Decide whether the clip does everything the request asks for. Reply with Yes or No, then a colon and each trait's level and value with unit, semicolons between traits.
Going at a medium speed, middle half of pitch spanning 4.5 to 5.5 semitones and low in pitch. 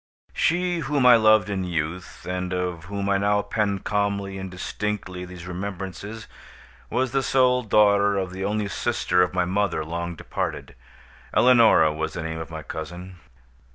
No: average, 160 wpm; average, 3.0 semitones; very low, 95 Hz